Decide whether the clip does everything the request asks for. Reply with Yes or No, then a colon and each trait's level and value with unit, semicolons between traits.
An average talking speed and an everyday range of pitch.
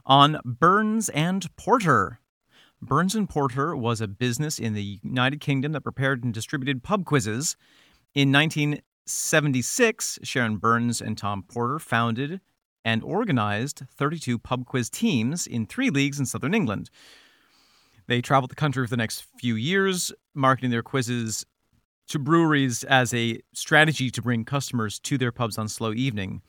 Yes: average, 150 wpm; average, 4.2 semitones